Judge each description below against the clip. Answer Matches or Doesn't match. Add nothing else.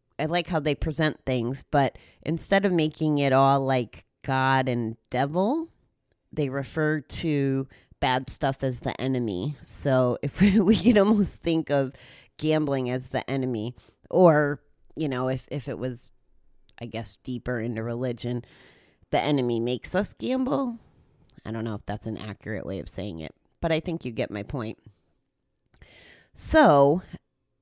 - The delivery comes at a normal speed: Matches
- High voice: Doesn't match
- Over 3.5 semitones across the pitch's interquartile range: Matches